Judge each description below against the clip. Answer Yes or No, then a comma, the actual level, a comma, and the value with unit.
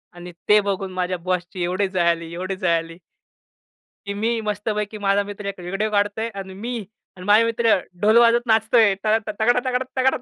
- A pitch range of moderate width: Yes, average, 3.3 semitones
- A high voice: Yes, high, 205 Hz